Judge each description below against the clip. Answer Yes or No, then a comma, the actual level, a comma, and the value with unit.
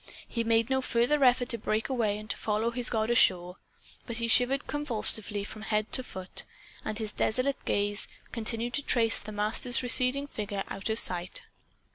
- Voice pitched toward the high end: Yes, high, 225 Hz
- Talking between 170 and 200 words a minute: Yes, average, 180 wpm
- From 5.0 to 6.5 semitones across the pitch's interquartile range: No, average, 2.8 semitones